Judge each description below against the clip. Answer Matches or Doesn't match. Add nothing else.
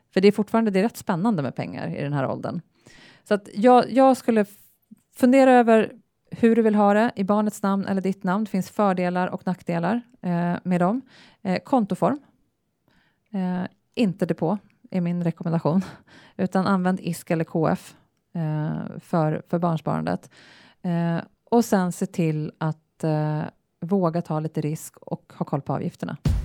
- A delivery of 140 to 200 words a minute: Matches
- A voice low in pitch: Doesn't match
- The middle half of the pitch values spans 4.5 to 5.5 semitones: Doesn't match